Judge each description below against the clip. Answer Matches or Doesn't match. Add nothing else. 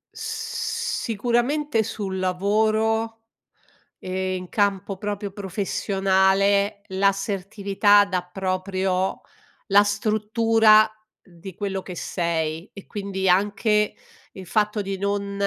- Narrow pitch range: Matches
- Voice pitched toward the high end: Matches